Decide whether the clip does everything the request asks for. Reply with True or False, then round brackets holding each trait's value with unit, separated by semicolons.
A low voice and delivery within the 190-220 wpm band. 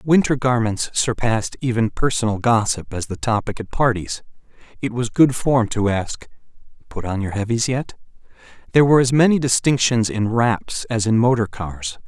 False (115 Hz; 165 wpm)